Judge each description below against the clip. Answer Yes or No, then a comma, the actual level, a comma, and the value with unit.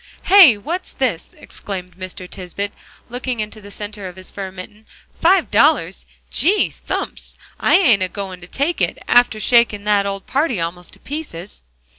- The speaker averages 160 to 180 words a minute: Yes, average, 165 wpm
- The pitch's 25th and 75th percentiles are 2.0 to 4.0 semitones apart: No, average, 5.2 semitones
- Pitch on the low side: No, high, 205 Hz